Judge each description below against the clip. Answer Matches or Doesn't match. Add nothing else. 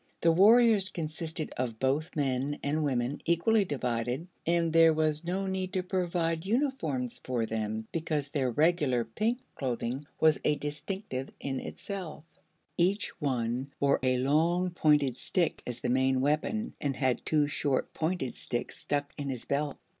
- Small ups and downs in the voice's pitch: Doesn't match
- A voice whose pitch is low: Doesn't match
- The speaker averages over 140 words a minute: Matches